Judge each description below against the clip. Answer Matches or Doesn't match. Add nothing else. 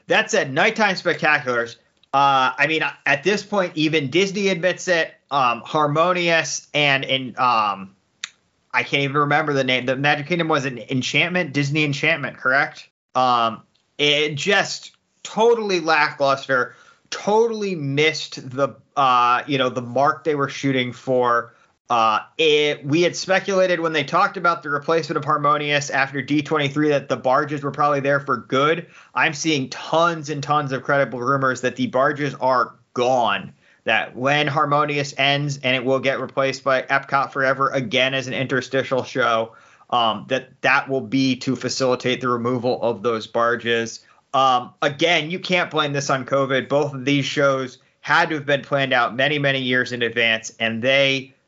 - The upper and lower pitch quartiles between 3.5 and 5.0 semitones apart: Doesn't match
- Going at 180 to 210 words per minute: Doesn't match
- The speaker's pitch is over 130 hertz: Matches